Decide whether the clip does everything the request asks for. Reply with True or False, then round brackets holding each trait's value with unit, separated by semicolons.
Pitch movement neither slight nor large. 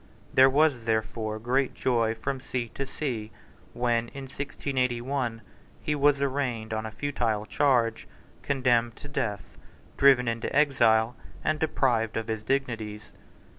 True (3.5 semitones)